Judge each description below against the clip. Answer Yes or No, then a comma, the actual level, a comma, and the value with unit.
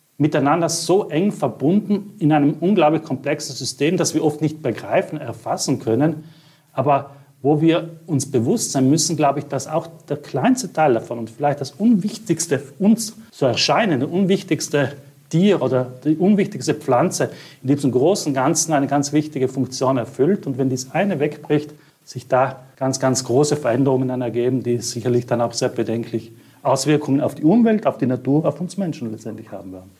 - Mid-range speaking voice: Yes, medium, 145 Hz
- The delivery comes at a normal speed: Yes, average, 170 wpm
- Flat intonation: No, average, 3.8 semitones